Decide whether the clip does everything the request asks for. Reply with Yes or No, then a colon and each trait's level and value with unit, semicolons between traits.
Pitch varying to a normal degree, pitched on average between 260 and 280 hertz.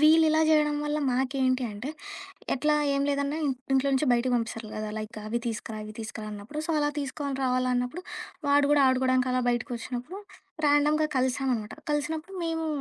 Yes: average, 3.3 semitones; very high, 265 Hz